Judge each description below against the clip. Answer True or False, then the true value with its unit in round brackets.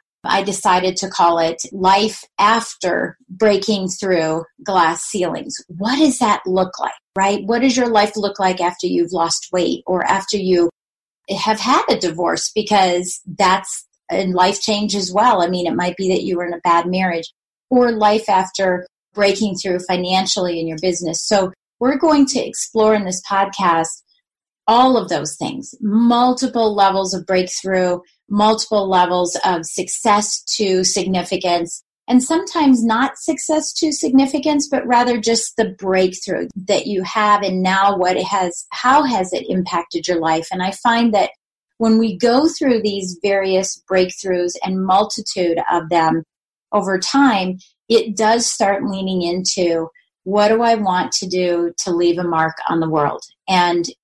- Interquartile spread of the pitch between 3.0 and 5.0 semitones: True (3.5 semitones)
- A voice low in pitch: False (190 Hz)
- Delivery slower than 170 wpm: True (160 wpm)